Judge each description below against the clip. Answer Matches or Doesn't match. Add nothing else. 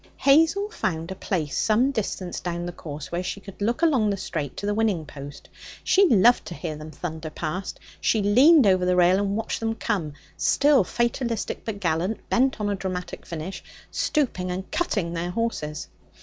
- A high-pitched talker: Matches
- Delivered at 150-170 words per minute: Doesn't match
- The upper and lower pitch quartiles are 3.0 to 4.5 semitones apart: Doesn't match